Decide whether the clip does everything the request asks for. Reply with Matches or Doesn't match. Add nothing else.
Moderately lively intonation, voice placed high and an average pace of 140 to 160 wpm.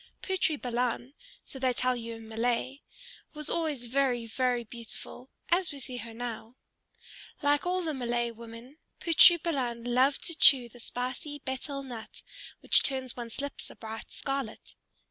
Matches